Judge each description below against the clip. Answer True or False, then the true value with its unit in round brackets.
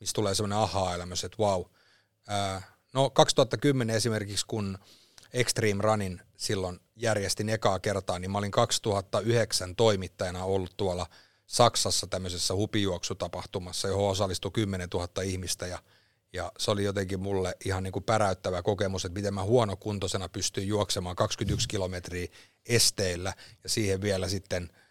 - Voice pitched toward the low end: True (100 Hz)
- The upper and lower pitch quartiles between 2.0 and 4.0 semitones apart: True (2.7 semitones)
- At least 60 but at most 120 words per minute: False (135 wpm)